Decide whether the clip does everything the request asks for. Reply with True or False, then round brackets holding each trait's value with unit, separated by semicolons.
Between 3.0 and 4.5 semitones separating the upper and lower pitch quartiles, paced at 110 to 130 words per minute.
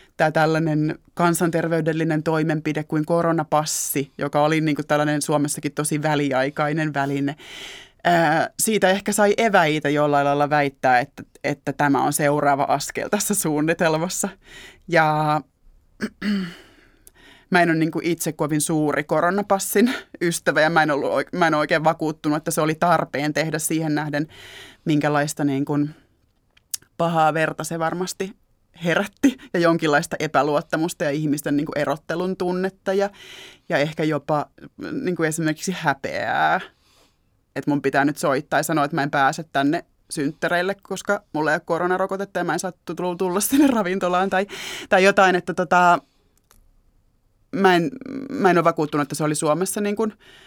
False (3.5 semitones; 145 wpm)